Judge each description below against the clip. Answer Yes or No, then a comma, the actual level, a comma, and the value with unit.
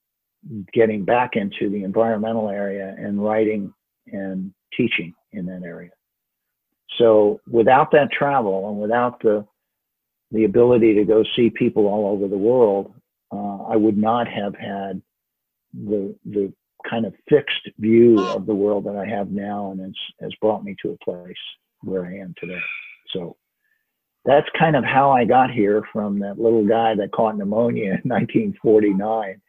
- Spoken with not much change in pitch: Yes, narrow, 2.2 semitones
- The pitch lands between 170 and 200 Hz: No, low, 105 Hz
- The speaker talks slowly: No, average, 165 wpm